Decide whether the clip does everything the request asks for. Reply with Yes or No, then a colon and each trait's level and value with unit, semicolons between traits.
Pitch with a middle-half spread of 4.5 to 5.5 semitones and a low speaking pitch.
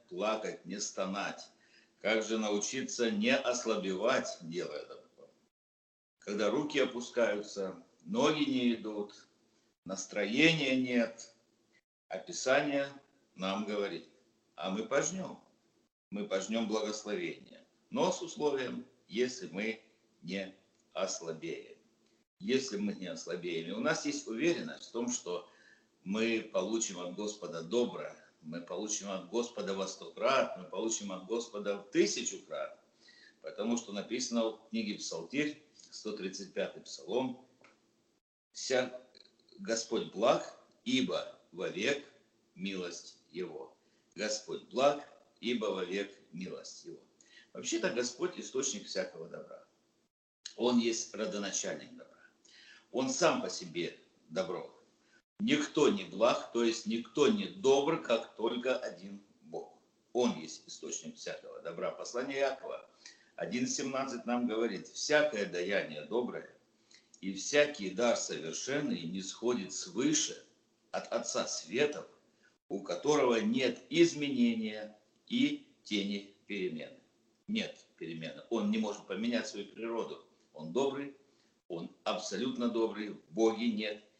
Yes: average, 4.8 semitones; low, 115 Hz